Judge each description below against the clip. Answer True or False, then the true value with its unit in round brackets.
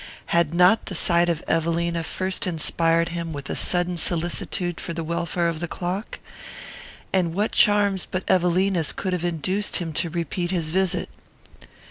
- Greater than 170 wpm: False (160 wpm)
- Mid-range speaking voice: True (175 Hz)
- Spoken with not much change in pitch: True (1.8 semitones)